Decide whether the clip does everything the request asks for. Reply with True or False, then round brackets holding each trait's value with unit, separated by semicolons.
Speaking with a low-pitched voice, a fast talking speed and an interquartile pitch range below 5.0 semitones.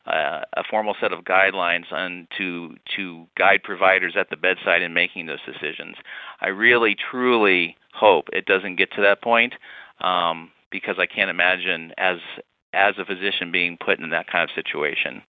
False (90 Hz; 170 wpm; 2.5 semitones)